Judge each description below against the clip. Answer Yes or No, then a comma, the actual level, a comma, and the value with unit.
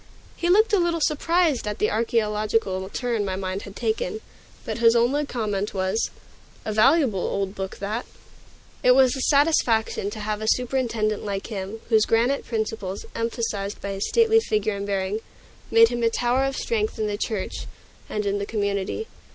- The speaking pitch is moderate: No, high, 220 Hz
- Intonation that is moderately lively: Yes, average, 3.6 semitones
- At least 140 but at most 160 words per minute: No, average, 175 wpm